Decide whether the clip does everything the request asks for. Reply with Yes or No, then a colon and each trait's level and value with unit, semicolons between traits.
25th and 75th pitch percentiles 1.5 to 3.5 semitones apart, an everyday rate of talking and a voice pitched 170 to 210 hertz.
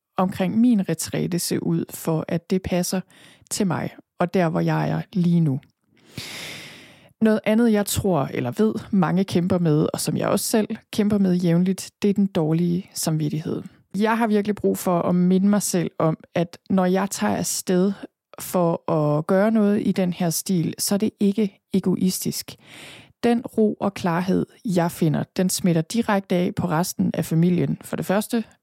Yes: average, 3.2 semitones; average, 180 wpm; medium, 185 Hz